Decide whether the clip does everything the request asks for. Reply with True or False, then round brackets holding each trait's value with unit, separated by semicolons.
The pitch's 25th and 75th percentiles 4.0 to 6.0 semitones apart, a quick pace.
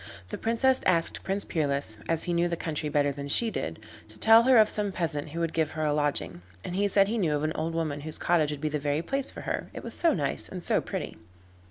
True (5.0 semitones; 260 wpm)